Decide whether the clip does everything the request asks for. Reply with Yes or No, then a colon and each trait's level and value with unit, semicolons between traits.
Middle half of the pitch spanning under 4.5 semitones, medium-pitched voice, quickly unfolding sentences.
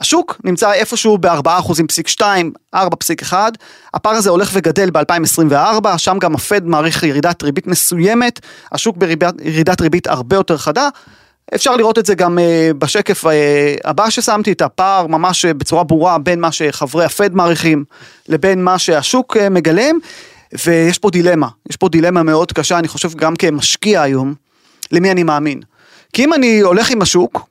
Yes: average, 4.1 semitones; medium, 175 Hz; fast, 155 wpm